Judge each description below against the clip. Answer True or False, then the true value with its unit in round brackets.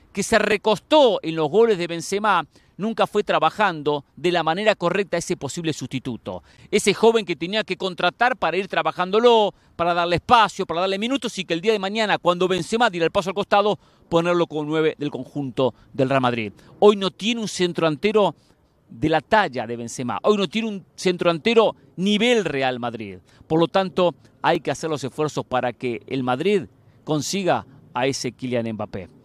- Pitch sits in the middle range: True (170 Hz)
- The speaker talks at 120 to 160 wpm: False (185 wpm)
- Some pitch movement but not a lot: False (6.9 semitones)